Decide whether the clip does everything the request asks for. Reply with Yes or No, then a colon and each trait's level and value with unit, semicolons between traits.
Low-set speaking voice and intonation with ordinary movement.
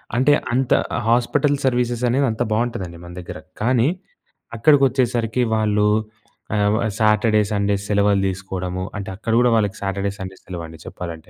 Yes: low, 110 Hz; average, 4.0 semitones